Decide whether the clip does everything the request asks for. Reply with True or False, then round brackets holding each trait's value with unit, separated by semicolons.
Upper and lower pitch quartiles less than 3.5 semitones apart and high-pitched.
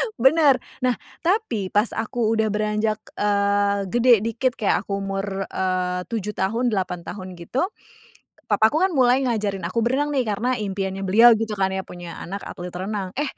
False (3.8 semitones; 210 Hz)